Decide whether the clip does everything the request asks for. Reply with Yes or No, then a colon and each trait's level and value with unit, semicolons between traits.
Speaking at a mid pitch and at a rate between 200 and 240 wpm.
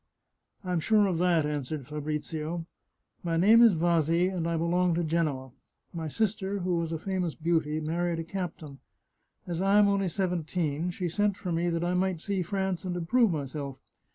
No: medium, 170 Hz; average, 185 wpm